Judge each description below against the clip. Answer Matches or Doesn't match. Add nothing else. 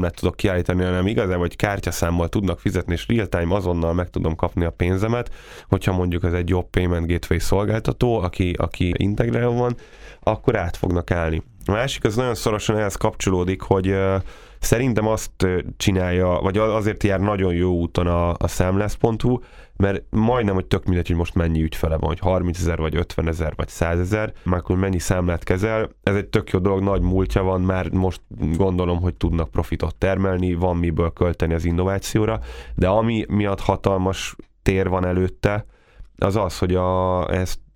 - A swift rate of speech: Matches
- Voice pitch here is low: Matches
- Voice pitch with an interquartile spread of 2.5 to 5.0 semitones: Matches